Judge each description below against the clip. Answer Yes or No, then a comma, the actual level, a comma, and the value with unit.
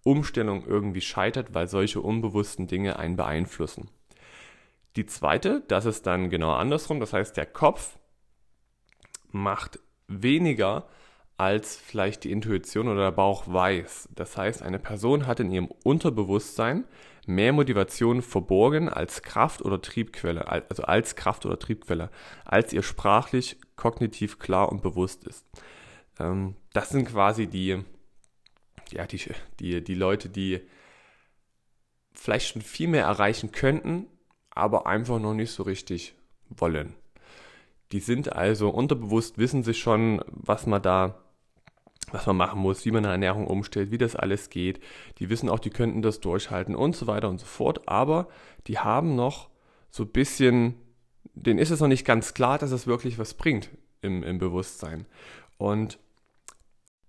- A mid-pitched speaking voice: No, low, 105 Hz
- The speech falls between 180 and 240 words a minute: No, average, 150 wpm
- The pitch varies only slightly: No, average, 3.8 semitones